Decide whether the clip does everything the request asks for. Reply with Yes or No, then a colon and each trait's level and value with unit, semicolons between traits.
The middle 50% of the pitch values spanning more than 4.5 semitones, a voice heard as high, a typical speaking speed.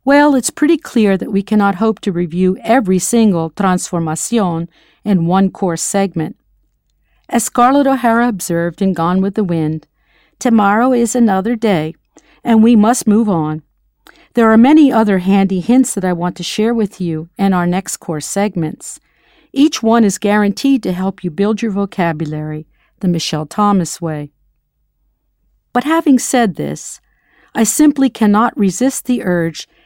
Yes: average, 5.2 semitones; high, 200 Hz; average, 155 wpm